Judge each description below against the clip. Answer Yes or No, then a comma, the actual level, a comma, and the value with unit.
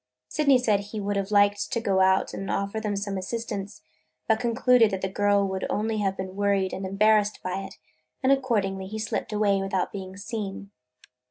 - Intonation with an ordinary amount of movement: No, narrow, 2.0 semitones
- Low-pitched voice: No, high, 200 Hz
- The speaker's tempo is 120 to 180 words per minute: No, average, 190 wpm